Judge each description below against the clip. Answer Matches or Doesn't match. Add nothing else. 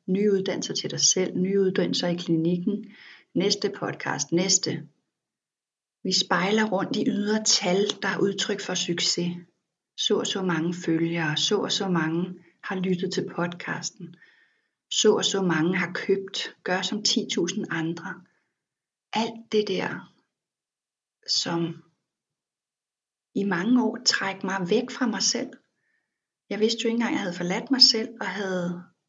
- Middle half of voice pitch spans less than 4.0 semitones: Matches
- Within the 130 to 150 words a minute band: Matches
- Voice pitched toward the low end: Doesn't match